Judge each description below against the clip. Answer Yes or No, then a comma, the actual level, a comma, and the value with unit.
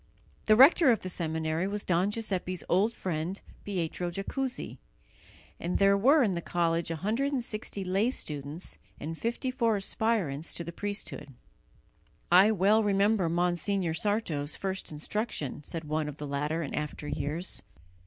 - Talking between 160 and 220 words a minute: No, average, 140 wpm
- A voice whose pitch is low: No, medium, 185 Hz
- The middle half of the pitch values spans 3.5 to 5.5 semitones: Yes, average, 4.8 semitones